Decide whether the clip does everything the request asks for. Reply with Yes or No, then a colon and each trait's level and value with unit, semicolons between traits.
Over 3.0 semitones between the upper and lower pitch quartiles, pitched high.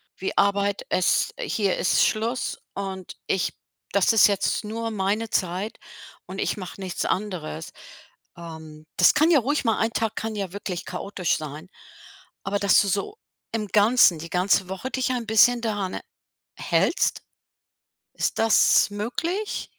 Yes: average, 3.4 semitones; high, 205 Hz